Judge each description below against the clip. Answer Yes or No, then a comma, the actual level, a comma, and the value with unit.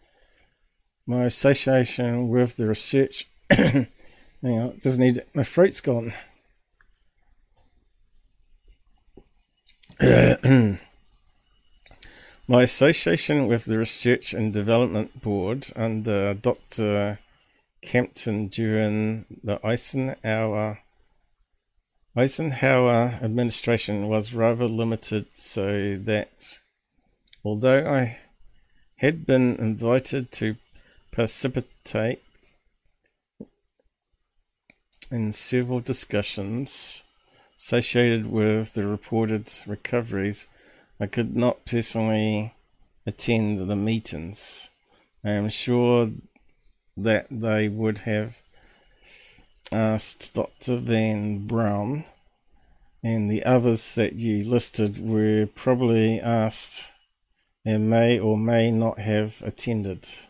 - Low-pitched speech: Yes, low, 115 Hz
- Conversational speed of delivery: No, slow, 80 wpm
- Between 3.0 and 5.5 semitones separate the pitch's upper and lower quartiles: No, narrow, 2.5 semitones